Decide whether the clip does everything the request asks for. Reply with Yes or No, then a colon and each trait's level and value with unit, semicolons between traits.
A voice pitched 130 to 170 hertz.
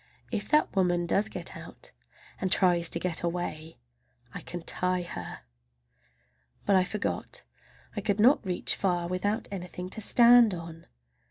No: medium, 185 Hz